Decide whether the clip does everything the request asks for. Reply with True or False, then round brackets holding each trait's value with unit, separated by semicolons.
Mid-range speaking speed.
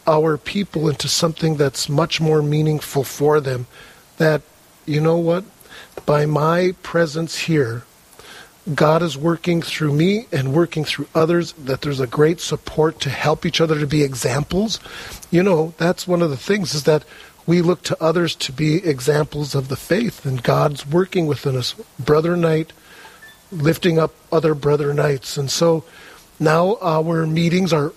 True (165 wpm)